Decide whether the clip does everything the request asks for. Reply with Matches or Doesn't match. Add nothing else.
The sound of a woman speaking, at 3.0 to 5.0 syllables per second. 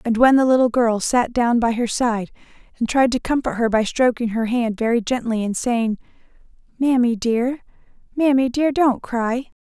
Matches